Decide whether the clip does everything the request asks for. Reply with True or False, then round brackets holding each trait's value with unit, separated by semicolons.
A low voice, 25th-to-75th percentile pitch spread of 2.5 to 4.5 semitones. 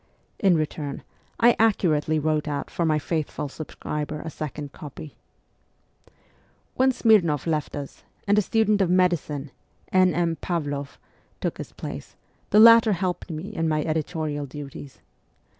False (160 Hz; 3.9 semitones)